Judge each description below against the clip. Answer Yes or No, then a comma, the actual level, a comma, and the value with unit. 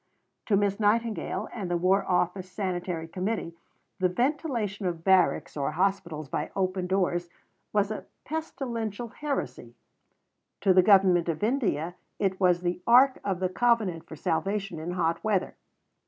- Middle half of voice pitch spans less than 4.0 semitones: Yes, average, 3.4 semitones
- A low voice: No, high, 190 Hz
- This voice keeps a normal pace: Yes, average, 145 wpm